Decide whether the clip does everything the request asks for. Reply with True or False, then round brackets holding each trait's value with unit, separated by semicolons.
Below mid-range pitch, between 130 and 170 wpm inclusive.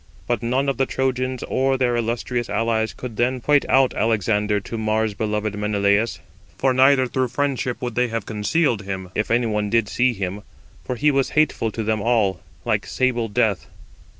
False (115 Hz; 180 wpm)